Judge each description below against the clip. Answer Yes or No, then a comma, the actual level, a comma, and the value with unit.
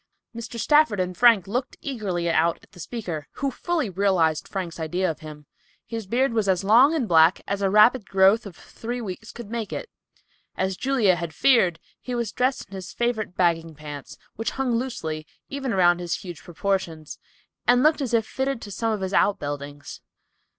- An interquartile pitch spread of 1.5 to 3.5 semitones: No, wide, 5.5 semitones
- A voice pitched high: Yes, high, 200 Hz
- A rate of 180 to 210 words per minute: Yes, average, 185 wpm